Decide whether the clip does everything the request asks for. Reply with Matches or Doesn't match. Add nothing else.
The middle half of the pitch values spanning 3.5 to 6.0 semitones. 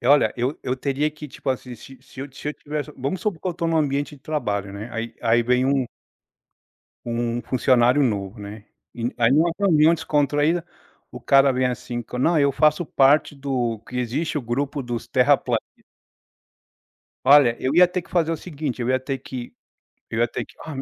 Matches